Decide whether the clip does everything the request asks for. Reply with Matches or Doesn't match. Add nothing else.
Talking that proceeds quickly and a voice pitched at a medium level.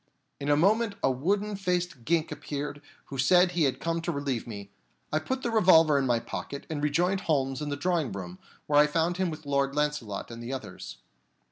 Matches